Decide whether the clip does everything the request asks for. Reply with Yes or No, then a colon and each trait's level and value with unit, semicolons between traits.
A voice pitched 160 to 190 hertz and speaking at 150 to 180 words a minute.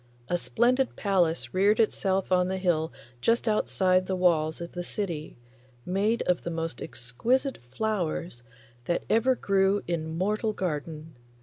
No: medium, 185 Hz; average, 140 wpm